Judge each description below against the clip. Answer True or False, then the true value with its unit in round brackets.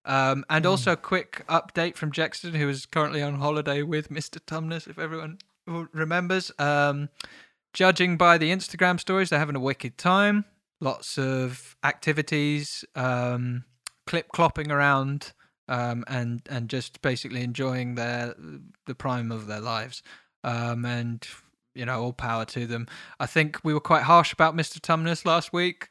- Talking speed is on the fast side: False (160 wpm)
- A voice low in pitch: False (145 Hz)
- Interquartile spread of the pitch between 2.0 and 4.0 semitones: False (4.8 semitones)